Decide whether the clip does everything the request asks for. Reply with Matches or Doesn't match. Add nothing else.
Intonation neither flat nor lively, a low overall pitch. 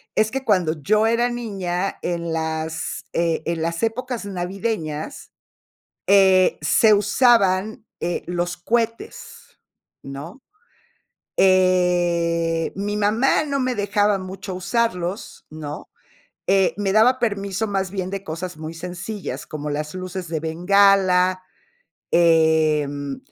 Doesn't match